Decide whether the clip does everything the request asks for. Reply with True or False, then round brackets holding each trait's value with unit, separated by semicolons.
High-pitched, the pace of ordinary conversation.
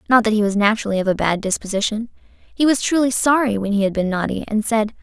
False (220 Hz; 240 wpm)